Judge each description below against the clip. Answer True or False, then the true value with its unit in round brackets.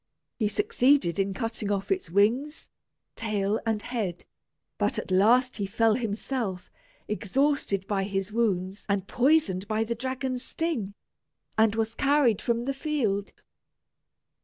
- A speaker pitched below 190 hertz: False (225 Hz)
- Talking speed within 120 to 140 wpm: True (135 wpm)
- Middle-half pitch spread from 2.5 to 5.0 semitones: True (4.5 semitones)